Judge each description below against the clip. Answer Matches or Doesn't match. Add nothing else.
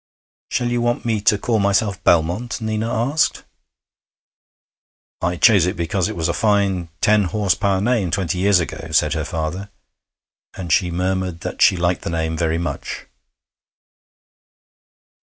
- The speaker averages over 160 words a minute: Doesn't match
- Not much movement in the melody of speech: Doesn't match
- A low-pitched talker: Matches